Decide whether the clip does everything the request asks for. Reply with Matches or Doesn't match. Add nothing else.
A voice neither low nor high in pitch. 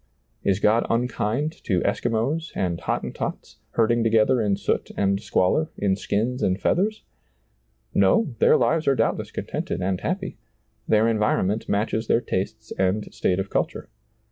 Doesn't match